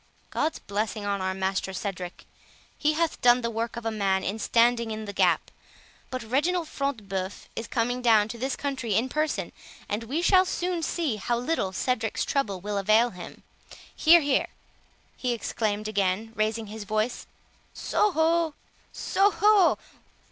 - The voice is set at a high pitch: Yes, high, 230 Hz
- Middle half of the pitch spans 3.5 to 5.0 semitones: No, wide, 5.5 semitones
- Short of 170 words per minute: Yes, average, 160 wpm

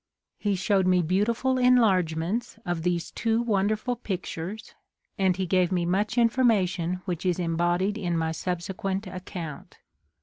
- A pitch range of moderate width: Yes, average, 3.4 semitones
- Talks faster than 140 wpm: No, slow, 135 wpm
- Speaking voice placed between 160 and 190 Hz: Yes, medium, 185 Hz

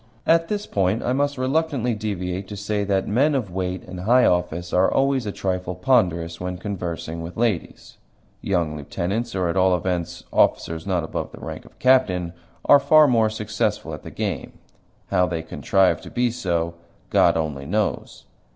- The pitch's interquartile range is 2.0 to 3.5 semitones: No, wide, 5.4 semitones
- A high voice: No, very low, 95 Hz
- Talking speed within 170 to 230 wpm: Yes, average, 175 wpm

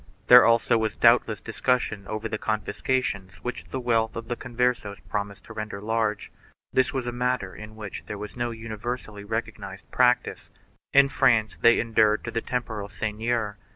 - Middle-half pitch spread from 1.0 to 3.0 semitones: Yes, narrow, 2.5 semitones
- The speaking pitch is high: No, low, 110 Hz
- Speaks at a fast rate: No, average, 170 wpm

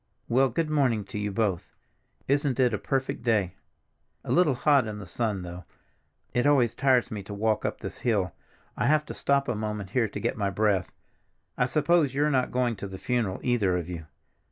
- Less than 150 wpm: No, fast, 205 wpm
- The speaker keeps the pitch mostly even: No, average, 4.7 semitones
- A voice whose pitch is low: Yes, low, 115 Hz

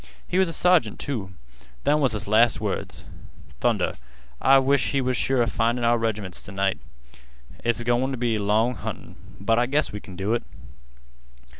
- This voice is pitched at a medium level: No, low, 120 Hz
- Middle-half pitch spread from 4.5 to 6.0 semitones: No, average, 3.7 semitones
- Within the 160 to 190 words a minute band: Yes, average, 180 wpm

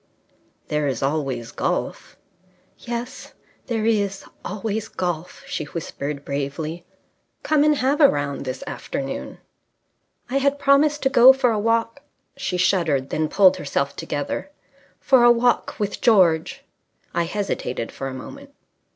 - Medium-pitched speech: No, high, 195 Hz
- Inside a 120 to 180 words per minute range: Yes, average, 140 wpm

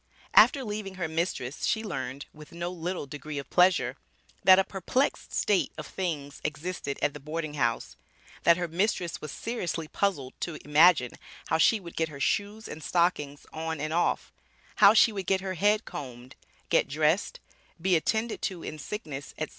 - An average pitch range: Yes, average, 4.4 semitones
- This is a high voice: No, medium, 165 Hz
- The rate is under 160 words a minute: No, average, 175 wpm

